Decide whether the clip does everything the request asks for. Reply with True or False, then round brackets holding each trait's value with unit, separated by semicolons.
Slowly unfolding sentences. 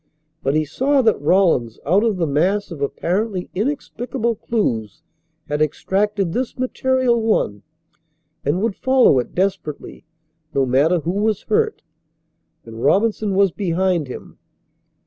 True (130 wpm)